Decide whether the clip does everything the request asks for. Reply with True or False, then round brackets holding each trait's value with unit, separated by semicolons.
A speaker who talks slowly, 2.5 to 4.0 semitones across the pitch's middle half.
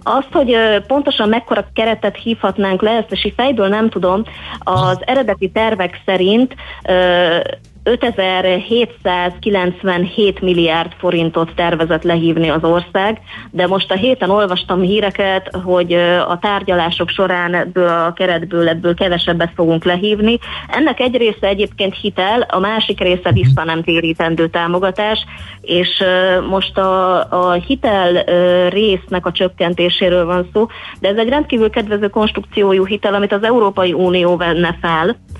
False (130 wpm; 2.9 semitones)